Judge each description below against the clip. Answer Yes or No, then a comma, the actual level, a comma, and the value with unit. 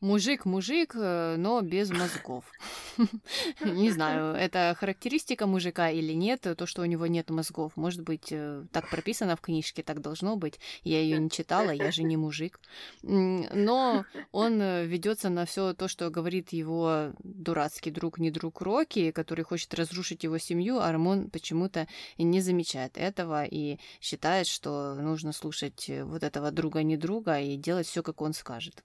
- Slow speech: No, average, 155 wpm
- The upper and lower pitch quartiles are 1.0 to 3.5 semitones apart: Yes, average, 3.0 semitones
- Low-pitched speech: No, medium, 170 Hz